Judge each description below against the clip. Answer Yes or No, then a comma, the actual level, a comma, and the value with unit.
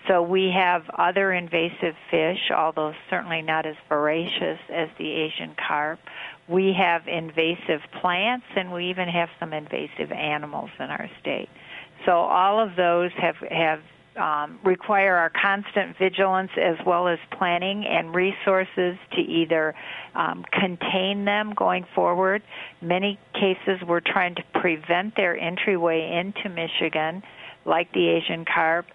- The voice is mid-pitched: Yes, medium, 175 Hz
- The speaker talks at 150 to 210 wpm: No, average, 140 wpm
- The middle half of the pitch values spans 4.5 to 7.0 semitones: No, narrow, 2.6 semitones